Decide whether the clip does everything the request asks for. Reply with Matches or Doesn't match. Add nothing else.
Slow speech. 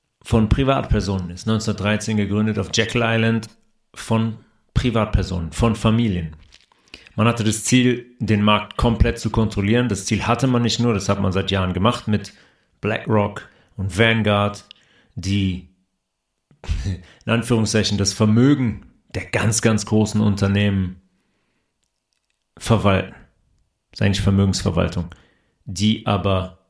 Matches